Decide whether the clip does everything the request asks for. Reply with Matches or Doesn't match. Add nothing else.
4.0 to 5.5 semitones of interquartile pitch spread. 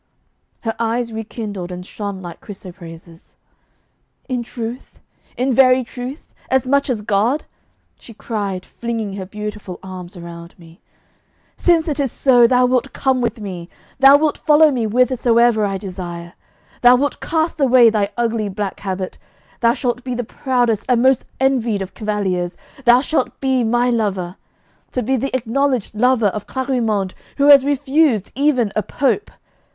Matches